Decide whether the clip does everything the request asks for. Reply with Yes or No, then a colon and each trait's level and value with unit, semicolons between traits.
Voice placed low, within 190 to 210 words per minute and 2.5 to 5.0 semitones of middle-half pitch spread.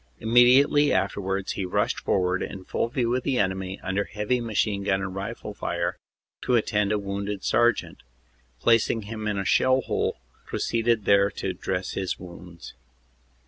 No: low, 100 Hz; average, 165 wpm; average, 3.5 semitones